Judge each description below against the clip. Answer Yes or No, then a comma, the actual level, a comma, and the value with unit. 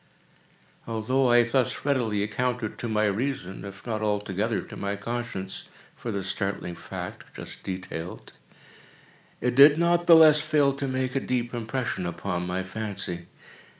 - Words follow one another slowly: No, average, 150 wpm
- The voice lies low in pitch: Yes, low, 110 Hz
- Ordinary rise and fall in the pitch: Yes, average, 4.8 semitones